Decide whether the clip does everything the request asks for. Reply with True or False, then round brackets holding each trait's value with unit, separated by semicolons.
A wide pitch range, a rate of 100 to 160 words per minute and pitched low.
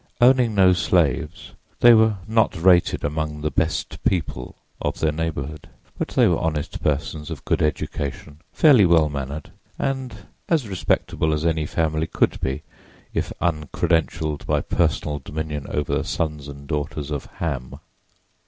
False (2.9 semitones; 145 wpm; 80 Hz)